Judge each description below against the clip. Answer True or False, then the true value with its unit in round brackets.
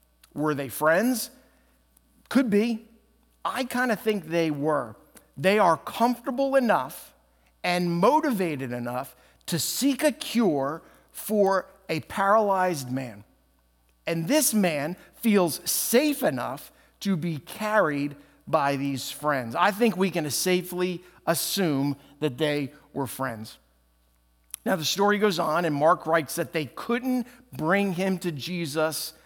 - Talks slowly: True (130 wpm)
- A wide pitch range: True (6.9 semitones)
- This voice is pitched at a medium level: True (170 Hz)